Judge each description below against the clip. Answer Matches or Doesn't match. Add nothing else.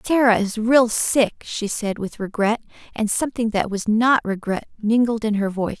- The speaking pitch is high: Matches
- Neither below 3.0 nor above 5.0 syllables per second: Matches